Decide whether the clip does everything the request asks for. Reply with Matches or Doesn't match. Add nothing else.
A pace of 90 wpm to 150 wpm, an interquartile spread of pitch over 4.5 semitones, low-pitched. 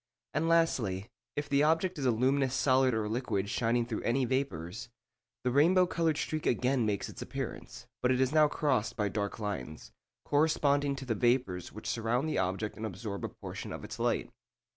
Doesn't match